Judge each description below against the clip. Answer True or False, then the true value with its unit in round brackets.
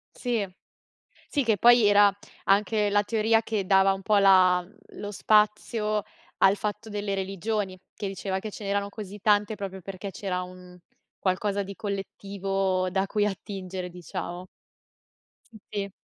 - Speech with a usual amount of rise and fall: False (1.7 semitones)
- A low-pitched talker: False (200 Hz)